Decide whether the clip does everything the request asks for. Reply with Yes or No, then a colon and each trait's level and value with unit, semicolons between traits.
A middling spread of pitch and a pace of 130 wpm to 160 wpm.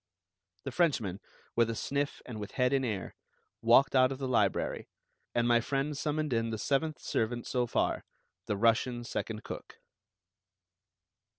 Yes: average, 3.2 semitones; average, 155 wpm